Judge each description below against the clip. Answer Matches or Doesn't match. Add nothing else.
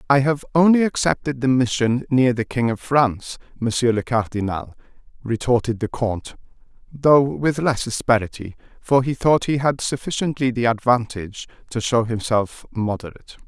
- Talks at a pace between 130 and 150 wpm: Matches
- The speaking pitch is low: Matches